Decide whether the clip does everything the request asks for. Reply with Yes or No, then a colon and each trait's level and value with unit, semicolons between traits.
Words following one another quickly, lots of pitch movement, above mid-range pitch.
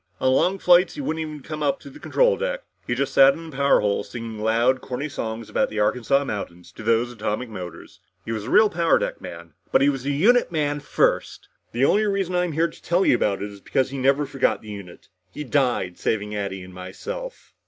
No: fast, 230 wpm; wide, 7.0 semitones; low, 135 Hz